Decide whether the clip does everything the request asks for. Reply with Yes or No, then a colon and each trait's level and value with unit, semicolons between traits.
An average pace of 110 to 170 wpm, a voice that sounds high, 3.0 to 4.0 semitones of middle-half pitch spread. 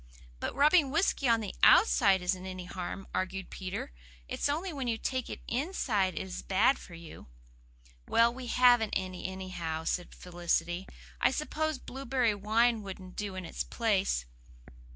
No: average, 155 wpm; high, 205 Hz; wide, 5.4 semitones